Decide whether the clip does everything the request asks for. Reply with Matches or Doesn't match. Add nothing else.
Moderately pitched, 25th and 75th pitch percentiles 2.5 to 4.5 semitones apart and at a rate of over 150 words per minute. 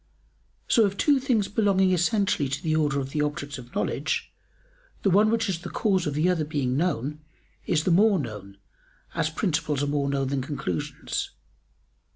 Doesn't match